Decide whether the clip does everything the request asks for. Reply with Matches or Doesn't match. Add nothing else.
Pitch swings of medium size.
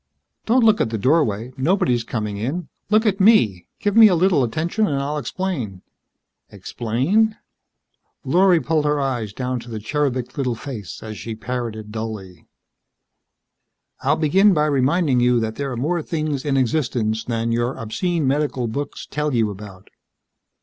Doesn't match